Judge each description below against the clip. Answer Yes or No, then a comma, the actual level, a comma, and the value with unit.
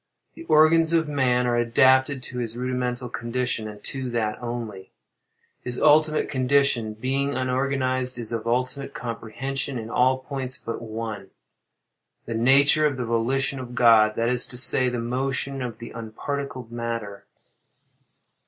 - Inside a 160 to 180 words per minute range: No, average, 140 wpm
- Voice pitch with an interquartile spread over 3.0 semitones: No, narrow, 2.5 semitones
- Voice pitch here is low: Yes, low, 125 Hz